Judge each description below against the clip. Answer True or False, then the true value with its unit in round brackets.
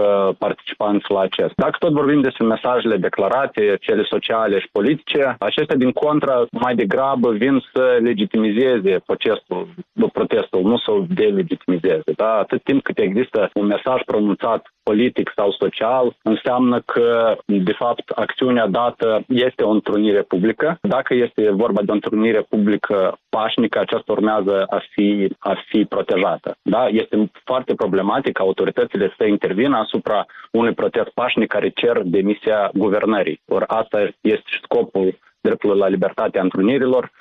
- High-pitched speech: False (120 Hz)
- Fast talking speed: False (140 wpm)